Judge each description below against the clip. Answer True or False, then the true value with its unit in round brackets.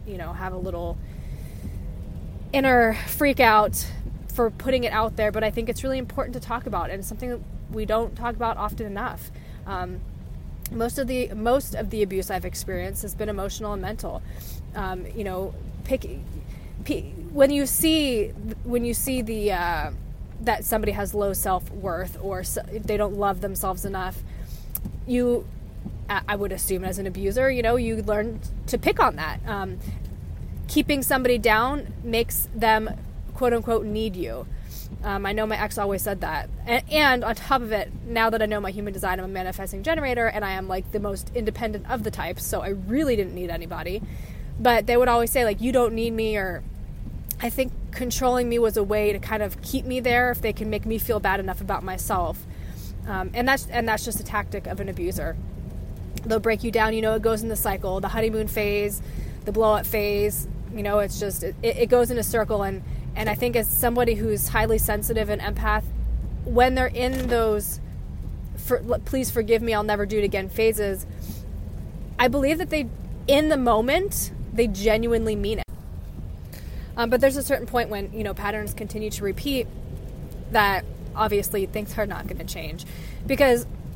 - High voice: True (220 Hz)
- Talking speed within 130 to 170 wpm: False (195 wpm)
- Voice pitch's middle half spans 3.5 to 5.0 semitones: False (3.0 semitones)